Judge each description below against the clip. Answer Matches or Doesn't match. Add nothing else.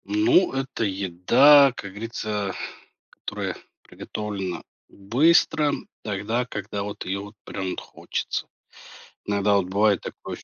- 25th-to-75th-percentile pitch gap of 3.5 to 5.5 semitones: Matches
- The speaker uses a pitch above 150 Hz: Doesn't match